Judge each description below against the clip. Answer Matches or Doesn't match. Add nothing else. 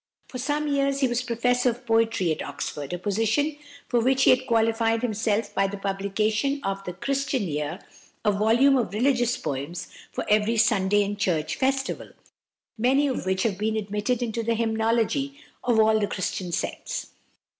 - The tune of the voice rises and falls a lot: Doesn't match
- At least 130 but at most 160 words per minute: Doesn't match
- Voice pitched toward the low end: Doesn't match